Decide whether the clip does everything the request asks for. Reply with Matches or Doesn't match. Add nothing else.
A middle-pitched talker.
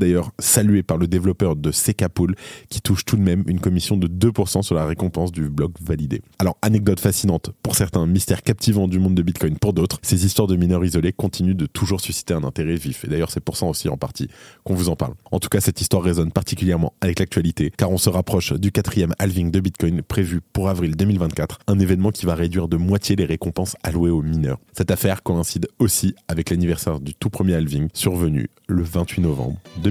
Doesn't match